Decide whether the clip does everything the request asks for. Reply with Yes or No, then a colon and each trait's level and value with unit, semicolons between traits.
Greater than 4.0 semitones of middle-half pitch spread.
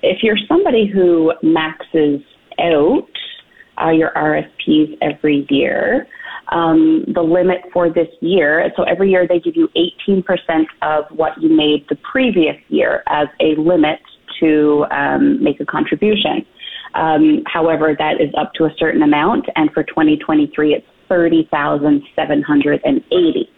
Yes: wide, 5.4 semitones